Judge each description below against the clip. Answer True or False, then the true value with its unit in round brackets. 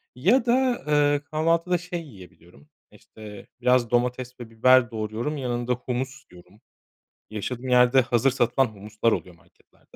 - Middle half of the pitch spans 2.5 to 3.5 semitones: False (4.6 semitones)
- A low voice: True (125 Hz)